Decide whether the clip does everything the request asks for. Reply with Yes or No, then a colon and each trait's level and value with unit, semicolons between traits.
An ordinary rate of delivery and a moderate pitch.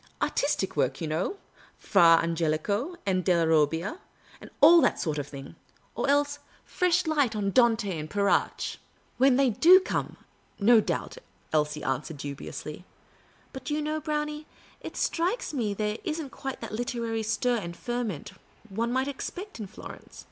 No: average, 175 wpm; high, 225 Hz